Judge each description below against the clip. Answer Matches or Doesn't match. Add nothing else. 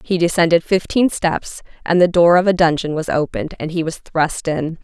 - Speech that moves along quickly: Matches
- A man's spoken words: Doesn't match